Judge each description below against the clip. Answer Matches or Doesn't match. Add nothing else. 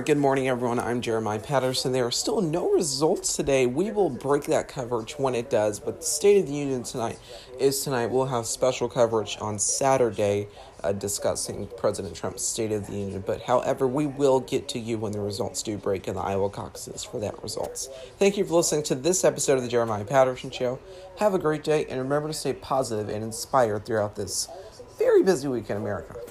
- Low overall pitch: Matches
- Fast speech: Matches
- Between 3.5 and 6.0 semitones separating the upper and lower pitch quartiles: Matches